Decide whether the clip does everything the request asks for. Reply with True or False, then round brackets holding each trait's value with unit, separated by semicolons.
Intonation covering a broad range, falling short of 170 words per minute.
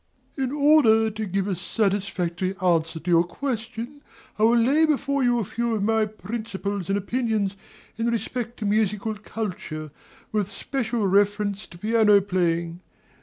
False (3.5 semitones; 155 wpm)